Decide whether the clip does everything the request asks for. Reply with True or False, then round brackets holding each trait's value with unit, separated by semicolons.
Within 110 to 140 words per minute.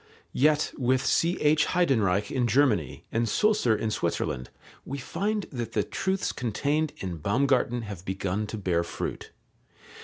True (135 wpm)